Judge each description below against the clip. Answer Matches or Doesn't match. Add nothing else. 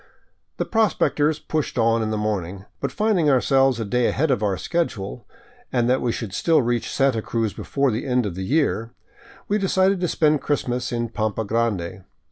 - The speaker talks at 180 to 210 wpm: Matches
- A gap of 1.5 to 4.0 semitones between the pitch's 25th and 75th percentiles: Doesn't match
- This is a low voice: Matches